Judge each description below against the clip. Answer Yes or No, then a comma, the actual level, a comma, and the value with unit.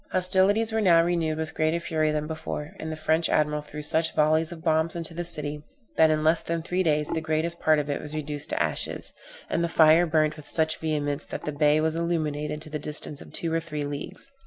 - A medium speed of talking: No, fast, 230 wpm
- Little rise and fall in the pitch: Yes, narrow, 1.7 semitones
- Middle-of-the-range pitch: Yes, medium, 155 Hz